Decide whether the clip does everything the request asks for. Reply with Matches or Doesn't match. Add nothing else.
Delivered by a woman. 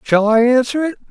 Doesn't match